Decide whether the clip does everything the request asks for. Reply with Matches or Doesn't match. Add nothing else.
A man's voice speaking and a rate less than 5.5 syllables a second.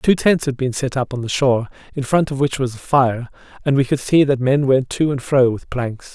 Matches